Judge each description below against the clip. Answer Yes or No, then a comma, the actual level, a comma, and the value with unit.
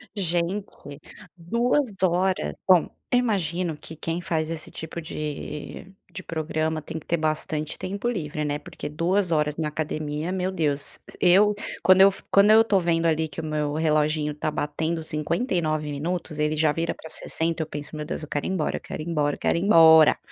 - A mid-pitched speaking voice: Yes, medium, 160 Hz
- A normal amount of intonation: Yes, average, 3.0 semitones